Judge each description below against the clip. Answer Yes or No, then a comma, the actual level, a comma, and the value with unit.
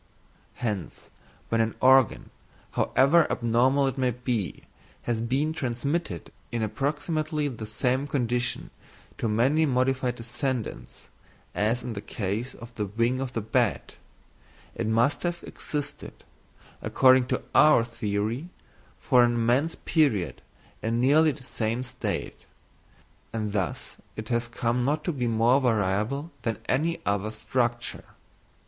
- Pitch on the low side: Yes, low, 120 Hz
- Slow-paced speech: Yes, slow, 130 wpm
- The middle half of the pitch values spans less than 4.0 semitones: Yes, average, 3.2 semitones